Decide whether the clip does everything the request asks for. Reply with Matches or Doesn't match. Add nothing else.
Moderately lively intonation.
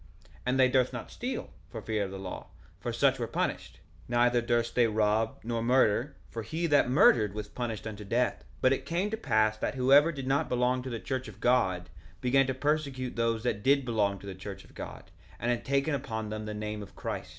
Matches